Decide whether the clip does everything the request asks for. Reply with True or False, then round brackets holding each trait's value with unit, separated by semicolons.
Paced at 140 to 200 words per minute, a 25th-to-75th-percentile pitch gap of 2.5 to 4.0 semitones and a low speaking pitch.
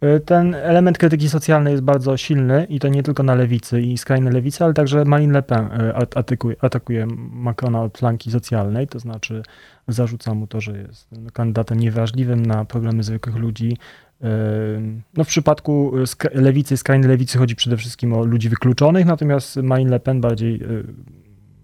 True (160 wpm; 3.5 semitones; 125 Hz)